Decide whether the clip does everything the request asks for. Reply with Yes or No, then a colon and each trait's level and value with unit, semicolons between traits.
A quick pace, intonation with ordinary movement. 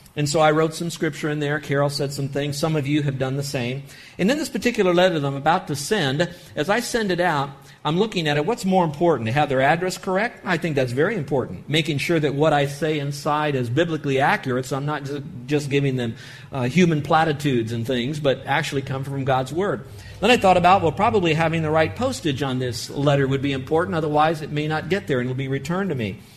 Yes: fast, 245 wpm; average, 3.5 semitones